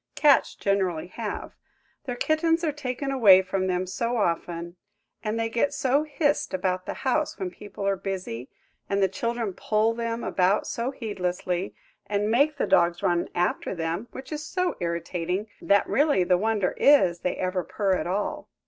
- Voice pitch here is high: Yes, high, 200 Hz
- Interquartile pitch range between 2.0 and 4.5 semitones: No, average, 5.2 semitones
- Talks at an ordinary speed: Yes, average, 165 wpm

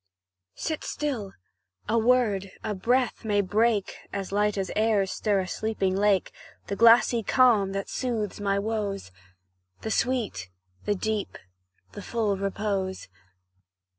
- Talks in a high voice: Yes, high, 210 Hz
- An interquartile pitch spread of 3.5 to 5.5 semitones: No, narrow, 2.5 semitones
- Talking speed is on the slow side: Yes, slow, 125 wpm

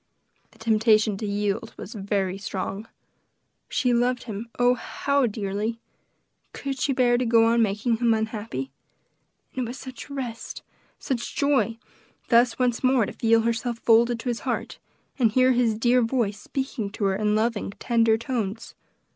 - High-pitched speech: Yes, high, 230 Hz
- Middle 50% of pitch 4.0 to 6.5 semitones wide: No, narrow, 2.5 semitones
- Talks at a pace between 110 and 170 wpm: Yes, average, 160 wpm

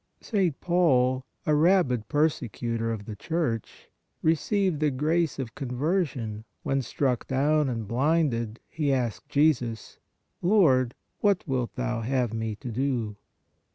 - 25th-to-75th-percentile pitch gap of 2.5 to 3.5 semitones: No, average, 5.0 semitones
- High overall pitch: No, low, 130 Hz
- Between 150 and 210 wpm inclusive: No, average, 140 wpm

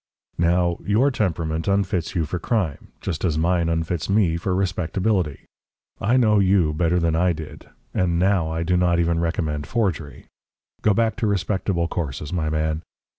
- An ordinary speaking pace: Yes, average, 165 wpm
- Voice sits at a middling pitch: No, very low, 85 Hz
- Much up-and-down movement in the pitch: No, average, 3.1 semitones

